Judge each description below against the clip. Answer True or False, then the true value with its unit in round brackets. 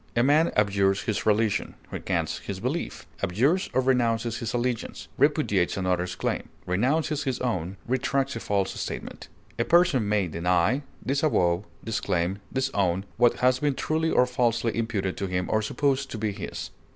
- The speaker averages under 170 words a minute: True (155 wpm)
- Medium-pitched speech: False (115 Hz)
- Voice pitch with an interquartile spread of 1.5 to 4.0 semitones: False (5.3 semitones)